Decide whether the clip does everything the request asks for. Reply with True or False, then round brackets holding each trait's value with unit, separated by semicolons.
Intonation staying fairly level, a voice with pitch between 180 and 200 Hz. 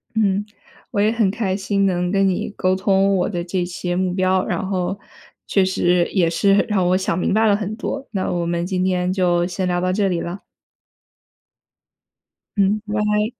True (2.1 semitones; 190 Hz)